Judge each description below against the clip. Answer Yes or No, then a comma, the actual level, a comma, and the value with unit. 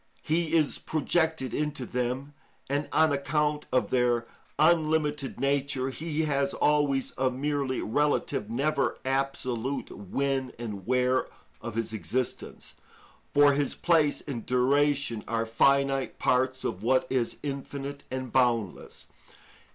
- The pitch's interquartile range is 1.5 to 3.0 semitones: Yes, narrow, 2.6 semitones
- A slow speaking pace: Yes, slow, 120 wpm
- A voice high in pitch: No, low, 135 Hz